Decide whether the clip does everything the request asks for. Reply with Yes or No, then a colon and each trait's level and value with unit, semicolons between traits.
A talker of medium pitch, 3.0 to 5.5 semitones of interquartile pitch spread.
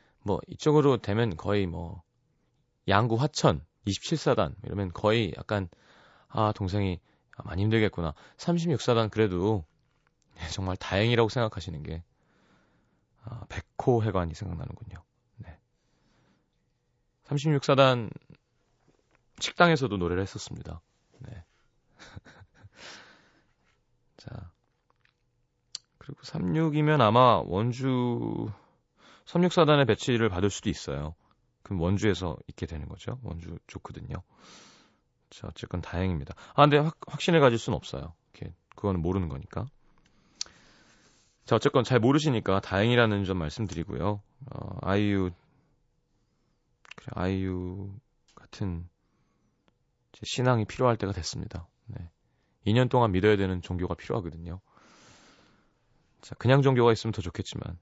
No: low, 105 Hz; average, 5.2 semitones